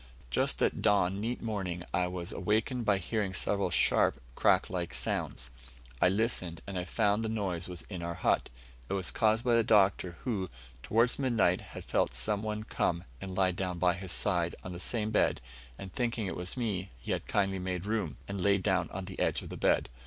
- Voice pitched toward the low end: Yes, very low, 95 Hz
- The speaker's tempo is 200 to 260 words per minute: Yes, fast, 205 wpm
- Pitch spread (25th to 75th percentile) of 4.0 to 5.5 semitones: No, average, 3.1 semitones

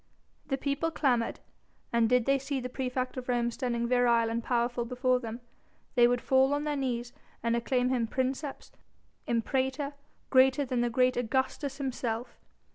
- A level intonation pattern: Yes, narrow, 2.0 semitones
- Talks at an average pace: Yes, average, 155 wpm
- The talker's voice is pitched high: Yes, very high, 250 Hz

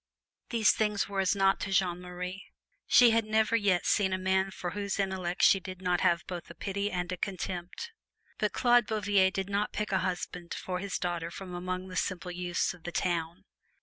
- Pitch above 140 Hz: Yes, high, 190 Hz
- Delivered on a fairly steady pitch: Yes, narrow, 2.0 semitones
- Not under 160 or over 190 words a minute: No, fast, 205 wpm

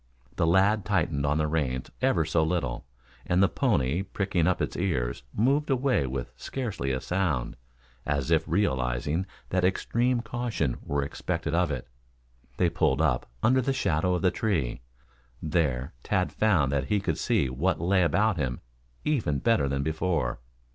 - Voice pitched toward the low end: Yes, very low, 85 Hz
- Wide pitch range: Yes, wide, 5.9 semitones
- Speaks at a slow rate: No, average, 160 wpm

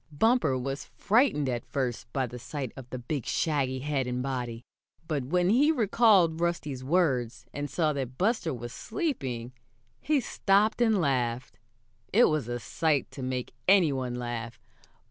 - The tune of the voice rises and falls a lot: Yes, wide, 6.3 semitones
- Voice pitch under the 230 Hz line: Yes, medium, 140 Hz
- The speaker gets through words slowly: No, average, 160 wpm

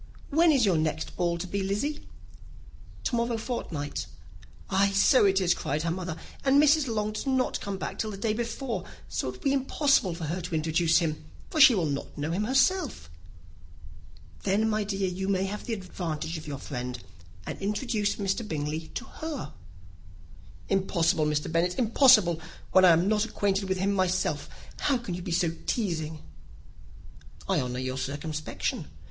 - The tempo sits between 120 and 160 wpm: No, average, 175 wpm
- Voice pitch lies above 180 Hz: Yes, high, 190 Hz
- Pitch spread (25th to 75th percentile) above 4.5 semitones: Yes, wide, 5.4 semitones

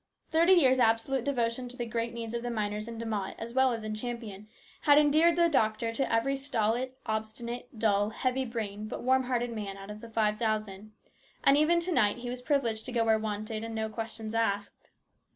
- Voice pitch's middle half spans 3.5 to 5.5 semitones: No, average, 2.9 semitones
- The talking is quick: Yes, fast, 210 wpm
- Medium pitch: No, high, 230 Hz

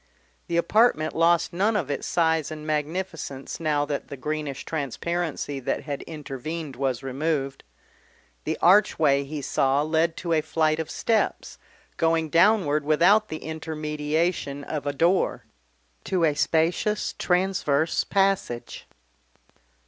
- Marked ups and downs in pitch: No, average, 2.9 semitones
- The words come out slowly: Yes, slow, 125 wpm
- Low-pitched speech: No, medium, 155 Hz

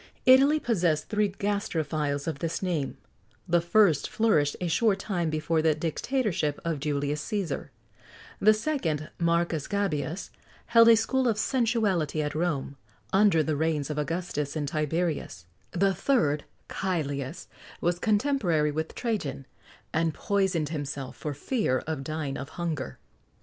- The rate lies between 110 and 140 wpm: Yes, slow, 135 wpm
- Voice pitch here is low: No, medium, 165 Hz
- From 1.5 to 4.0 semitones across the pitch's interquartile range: No, average, 5.2 semitones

